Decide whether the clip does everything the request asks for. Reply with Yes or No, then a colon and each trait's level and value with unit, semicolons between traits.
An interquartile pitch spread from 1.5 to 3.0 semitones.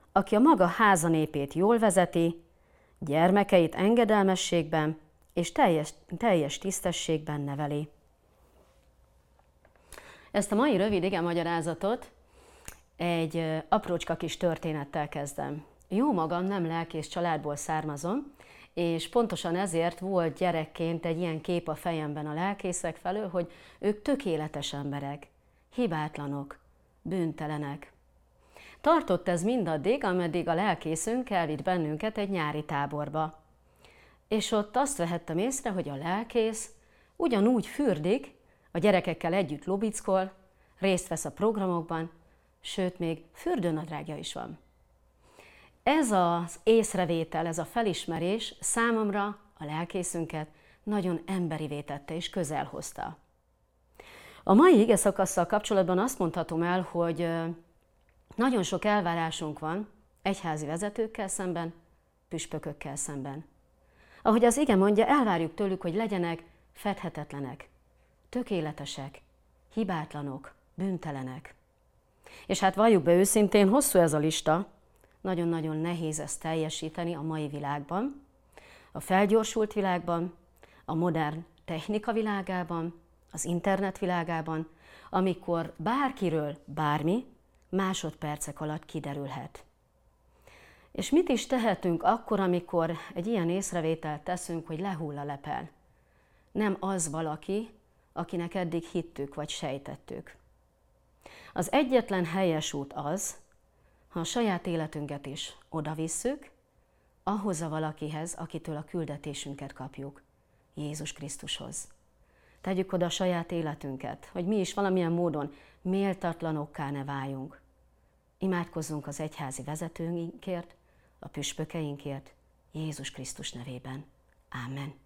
No: average, 4.2 semitones